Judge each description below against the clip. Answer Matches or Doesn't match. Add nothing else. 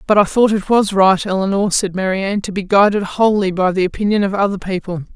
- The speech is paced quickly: Matches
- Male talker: Doesn't match